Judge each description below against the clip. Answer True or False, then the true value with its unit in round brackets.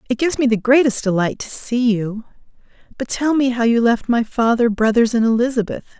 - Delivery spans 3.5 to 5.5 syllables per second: False (5.7 syllables/s)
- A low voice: False (235 Hz)